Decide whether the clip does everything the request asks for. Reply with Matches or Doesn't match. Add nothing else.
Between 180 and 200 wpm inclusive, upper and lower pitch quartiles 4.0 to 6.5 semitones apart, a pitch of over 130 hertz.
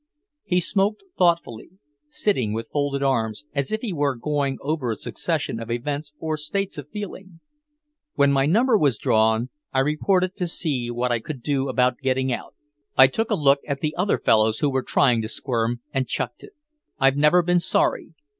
Matches